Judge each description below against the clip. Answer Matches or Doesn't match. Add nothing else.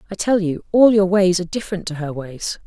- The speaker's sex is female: Matches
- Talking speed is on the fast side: Matches